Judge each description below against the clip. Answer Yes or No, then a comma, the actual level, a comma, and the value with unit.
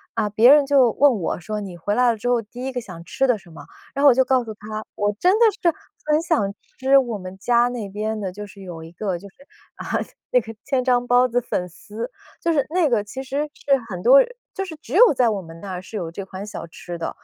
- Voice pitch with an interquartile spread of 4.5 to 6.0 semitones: Yes, average, 5.1 semitones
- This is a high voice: Yes, high, 225 Hz